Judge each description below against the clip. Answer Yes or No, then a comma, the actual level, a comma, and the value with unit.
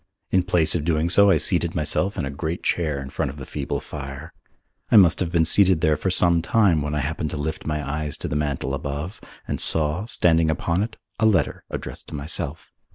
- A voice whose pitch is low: Yes, very low, 80 Hz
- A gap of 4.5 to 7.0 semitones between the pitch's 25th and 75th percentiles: No, average, 3.1 semitones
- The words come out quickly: Yes, fast, 225 wpm